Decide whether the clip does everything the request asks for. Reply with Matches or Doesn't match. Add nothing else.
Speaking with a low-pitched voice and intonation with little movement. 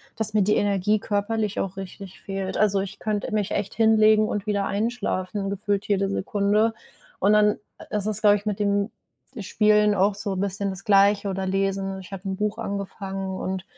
Doesn't match